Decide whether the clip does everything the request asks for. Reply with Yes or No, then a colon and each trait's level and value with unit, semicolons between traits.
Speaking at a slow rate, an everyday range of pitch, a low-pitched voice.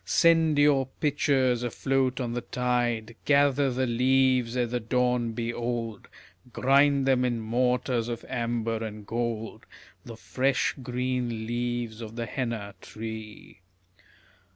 No: slow, 130 wpm; narrow, 2.1 semitones; low, 120 Hz